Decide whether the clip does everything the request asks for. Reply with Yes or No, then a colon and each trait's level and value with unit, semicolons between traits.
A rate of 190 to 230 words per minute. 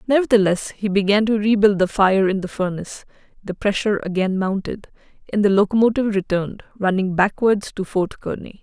No: average, 160 wpm